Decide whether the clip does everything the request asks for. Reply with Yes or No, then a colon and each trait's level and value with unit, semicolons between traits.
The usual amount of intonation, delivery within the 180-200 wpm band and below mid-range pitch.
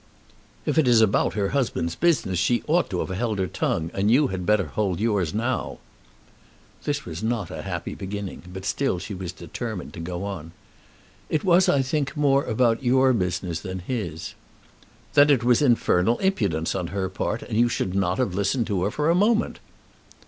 No: wide, 5.9 semitones; average, 190 wpm; low, 105 Hz